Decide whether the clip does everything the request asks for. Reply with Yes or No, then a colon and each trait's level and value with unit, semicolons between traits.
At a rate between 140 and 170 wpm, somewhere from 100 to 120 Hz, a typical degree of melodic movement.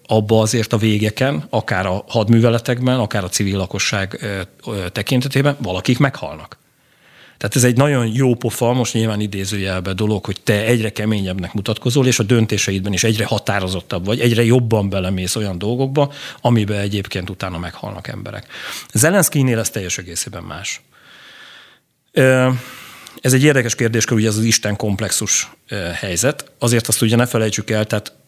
Yes: average, 145 wpm; low, 110 Hz; average, 3.4 semitones